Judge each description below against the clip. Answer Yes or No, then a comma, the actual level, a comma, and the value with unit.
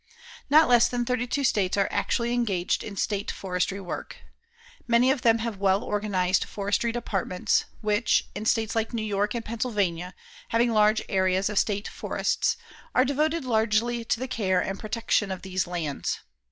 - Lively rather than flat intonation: No, average, 3.5 semitones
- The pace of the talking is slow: No, average, 165 wpm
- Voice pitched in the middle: No, high, 215 Hz